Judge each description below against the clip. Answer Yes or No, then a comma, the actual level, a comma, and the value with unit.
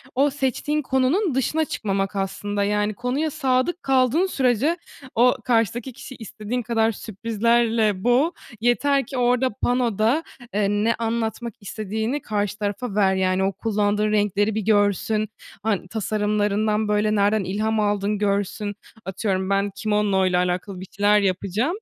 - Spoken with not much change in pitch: No, average, 3.2 semitones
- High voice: Yes, high, 215 Hz